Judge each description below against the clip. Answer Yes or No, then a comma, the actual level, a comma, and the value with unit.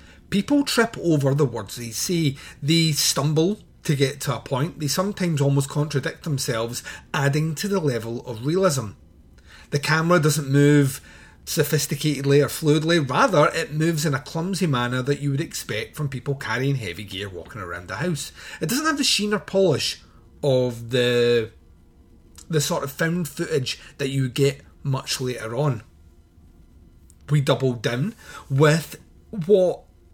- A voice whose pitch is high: No, medium, 140 Hz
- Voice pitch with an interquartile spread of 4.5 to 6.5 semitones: Yes, average, 5.2 semitones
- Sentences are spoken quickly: No, average, 155 wpm